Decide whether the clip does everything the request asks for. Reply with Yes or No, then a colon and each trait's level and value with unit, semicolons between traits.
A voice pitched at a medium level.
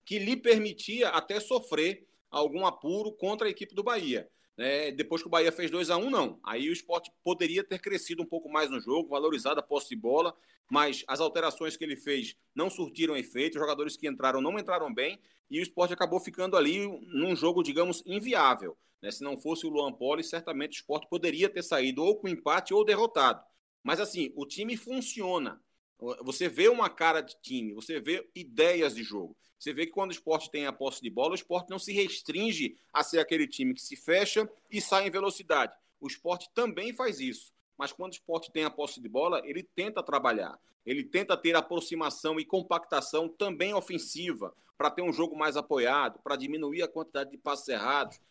Yes: medium, 170 Hz